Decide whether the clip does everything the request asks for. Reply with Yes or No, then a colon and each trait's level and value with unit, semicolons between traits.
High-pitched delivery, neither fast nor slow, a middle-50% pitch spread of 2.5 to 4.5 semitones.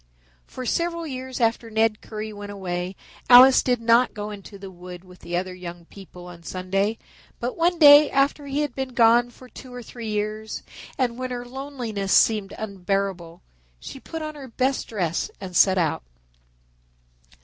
No: high, 220 Hz; average, 170 wpm; average, 5.1 semitones